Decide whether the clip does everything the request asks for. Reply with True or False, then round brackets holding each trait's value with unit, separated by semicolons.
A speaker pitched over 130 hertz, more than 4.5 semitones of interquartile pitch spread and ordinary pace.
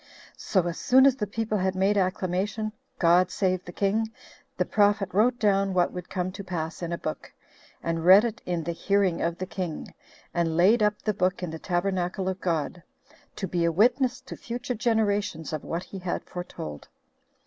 False (185 Hz; 3.1 semitones; 190 wpm)